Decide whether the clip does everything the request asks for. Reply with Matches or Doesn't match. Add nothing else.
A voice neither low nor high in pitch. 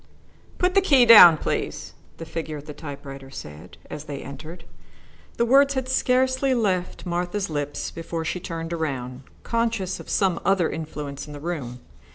Matches